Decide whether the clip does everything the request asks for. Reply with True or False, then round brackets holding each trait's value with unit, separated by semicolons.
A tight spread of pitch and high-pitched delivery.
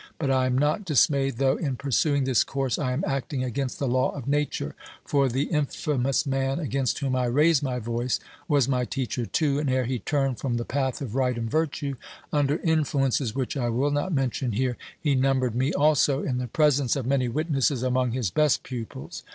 False (2.2 semitones; 135 Hz)